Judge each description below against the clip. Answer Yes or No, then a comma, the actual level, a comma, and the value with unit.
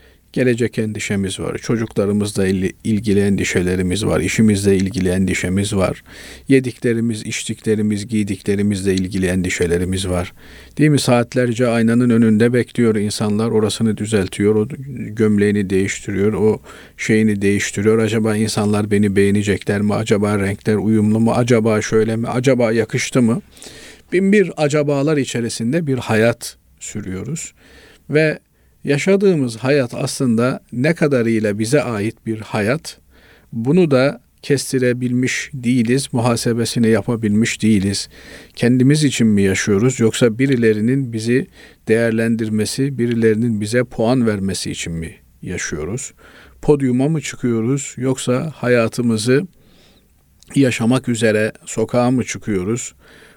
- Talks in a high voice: No, low, 110 Hz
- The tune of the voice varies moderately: Yes, average, 3.5 semitones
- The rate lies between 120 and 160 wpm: No, average, 110 wpm